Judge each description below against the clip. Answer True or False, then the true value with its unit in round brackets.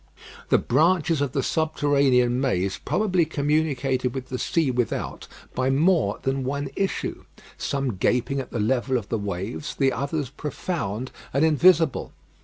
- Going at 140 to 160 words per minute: True (145 wpm)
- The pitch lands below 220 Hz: True (135 Hz)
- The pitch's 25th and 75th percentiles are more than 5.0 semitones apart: False (3.6 semitones)